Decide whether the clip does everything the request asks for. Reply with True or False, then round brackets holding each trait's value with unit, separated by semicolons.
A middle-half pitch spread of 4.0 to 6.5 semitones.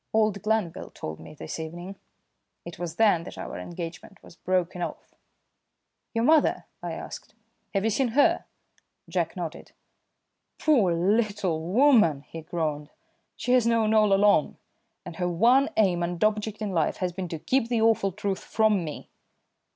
True (4.4 semitones)